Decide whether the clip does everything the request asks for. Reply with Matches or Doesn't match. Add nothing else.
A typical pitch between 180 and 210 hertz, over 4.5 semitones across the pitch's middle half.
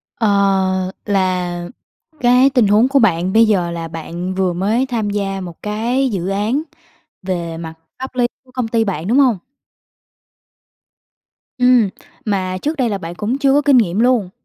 Matches